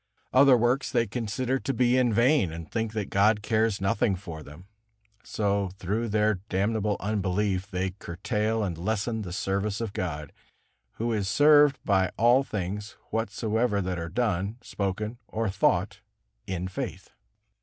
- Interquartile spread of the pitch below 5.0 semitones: Yes, average, 3.2 semitones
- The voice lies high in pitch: No, low, 105 Hz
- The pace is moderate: Yes, average, 150 wpm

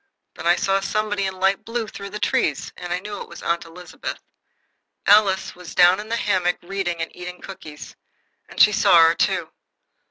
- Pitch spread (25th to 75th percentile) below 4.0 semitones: Yes, narrow, 2.6 semitones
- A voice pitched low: No, high, 190 Hz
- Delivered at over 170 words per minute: Yes, average, 190 wpm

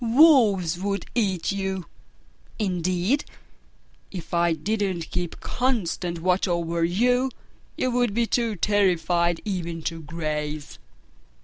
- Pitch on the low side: No, medium, 185 Hz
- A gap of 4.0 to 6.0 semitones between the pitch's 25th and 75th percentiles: Yes, average, 4.3 semitones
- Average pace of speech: No, slow, 110 wpm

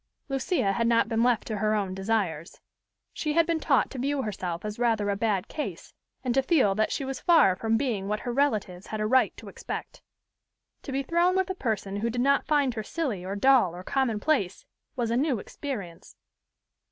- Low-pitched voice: No, high, 230 Hz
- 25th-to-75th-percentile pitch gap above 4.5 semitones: Yes, average, 5.1 semitones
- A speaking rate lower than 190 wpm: No, fast, 205 wpm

